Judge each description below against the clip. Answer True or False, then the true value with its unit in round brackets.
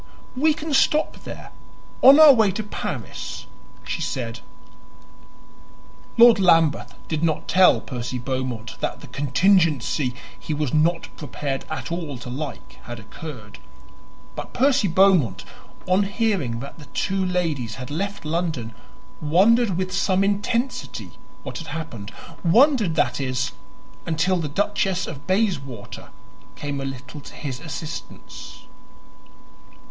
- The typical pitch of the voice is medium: True (165 Hz)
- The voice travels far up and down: True (6.4 semitones)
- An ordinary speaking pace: False (130 wpm)